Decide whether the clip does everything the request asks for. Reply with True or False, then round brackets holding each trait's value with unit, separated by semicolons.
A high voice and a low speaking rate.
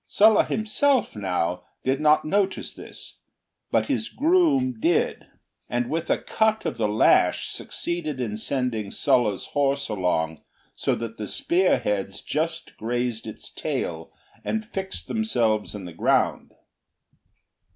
False (130 Hz; 130 wpm)